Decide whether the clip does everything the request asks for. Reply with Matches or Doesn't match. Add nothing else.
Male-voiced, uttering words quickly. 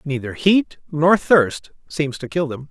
Doesn't match